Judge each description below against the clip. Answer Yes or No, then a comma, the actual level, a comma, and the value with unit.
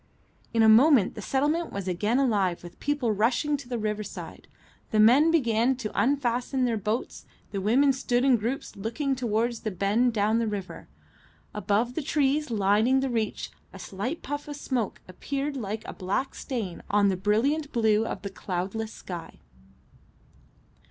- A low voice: No, high, 230 Hz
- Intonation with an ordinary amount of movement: Yes, average, 4.3 semitones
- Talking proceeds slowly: No, average, 165 wpm